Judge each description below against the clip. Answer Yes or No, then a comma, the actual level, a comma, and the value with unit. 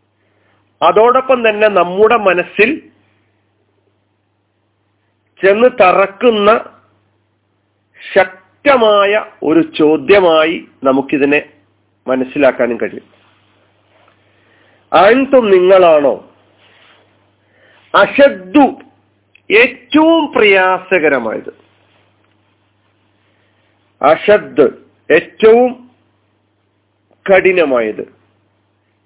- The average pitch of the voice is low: Yes, low, 110 Hz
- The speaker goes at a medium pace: No, slow, 40 wpm